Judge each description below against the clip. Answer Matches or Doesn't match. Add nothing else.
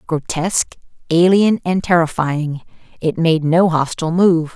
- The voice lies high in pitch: Doesn't match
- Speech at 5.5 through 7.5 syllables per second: Doesn't match